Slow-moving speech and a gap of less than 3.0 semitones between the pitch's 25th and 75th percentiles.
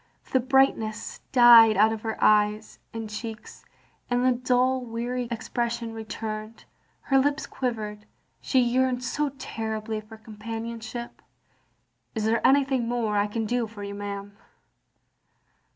Yes: slow, 130 wpm; narrow, 2.4 semitones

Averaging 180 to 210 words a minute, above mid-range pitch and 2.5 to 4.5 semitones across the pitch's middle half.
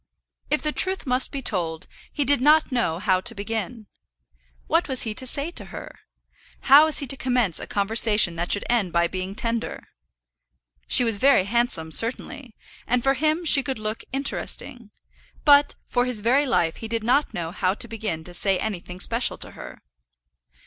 No: average, 185 wpm; high, 230 Hz; wide, 5.4 semitones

